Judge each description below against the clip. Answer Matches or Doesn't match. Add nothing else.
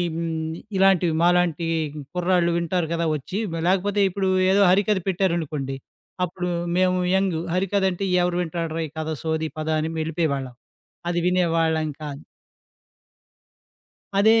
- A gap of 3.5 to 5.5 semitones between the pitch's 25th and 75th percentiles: Doesn't match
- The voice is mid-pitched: Matches